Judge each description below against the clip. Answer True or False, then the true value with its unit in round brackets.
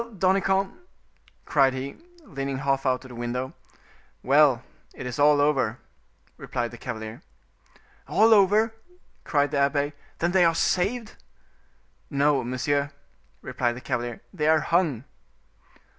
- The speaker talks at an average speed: False (130 wpm)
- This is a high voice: False (140 Hz)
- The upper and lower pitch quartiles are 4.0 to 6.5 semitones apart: True (5.1 semitones)